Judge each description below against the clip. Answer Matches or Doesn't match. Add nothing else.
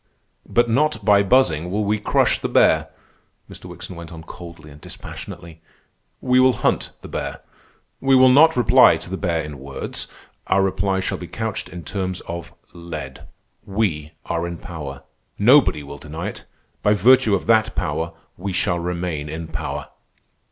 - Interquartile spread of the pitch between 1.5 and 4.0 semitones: Doesn't match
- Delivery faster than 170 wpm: Doesn't match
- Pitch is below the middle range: Matches